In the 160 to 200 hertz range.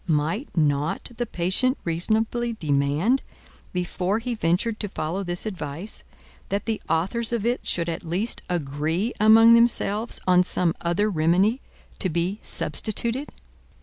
Yes: high, 190 Hz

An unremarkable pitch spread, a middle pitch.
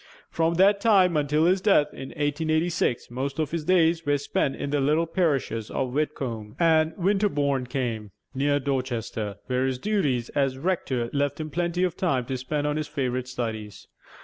Yes: average, 4.3 semitones; medium, 145 Hz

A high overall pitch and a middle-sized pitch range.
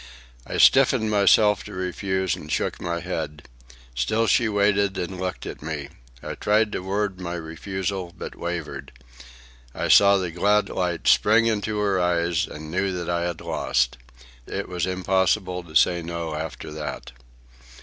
No: very low, 90 Hz; average, 3.2 semitones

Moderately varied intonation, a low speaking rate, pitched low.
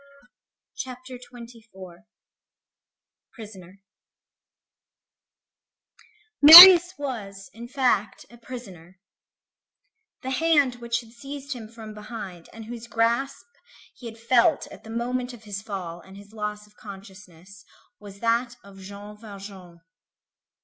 No: average, 3.7 semitones; slow, 110 wpm; high, 225 Hz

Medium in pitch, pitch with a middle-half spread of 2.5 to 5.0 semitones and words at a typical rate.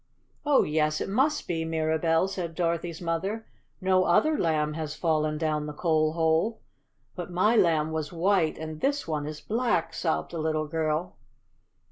Yes: medium, 165 Hz; average, 2.8 semitones; average, 160 wpm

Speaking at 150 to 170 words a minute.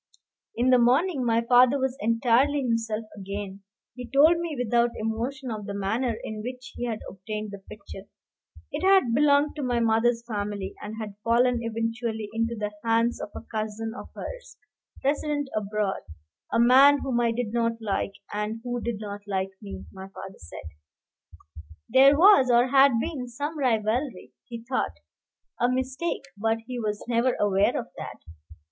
Yes: average, 165 wpm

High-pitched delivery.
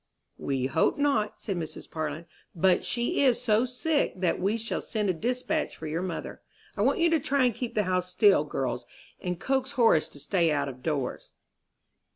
Yes: high, 200 Hz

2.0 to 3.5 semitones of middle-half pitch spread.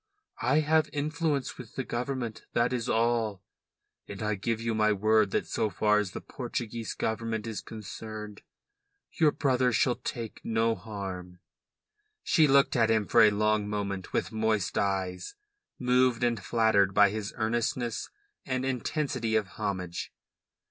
Yes: average, 2.9 semitones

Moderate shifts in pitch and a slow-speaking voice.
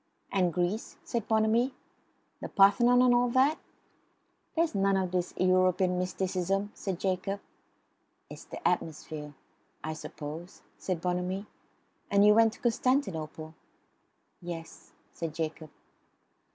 Yes: average, 4.0 semitones; slow, 115 wpm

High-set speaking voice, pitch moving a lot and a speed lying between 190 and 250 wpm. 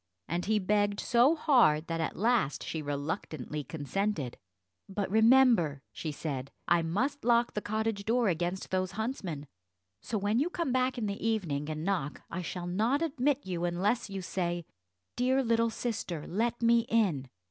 No: high, 200 Hz; wide, 5.9 semitones; average, 165 wpm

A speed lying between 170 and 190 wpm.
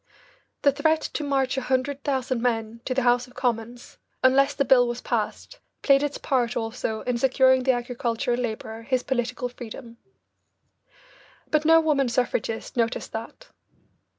No: average, 150 wpm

